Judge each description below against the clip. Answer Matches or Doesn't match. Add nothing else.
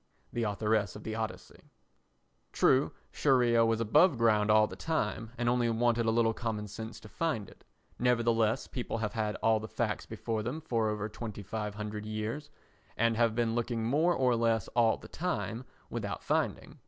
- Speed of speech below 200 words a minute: Matches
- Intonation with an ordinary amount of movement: Doesn't match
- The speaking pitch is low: Matches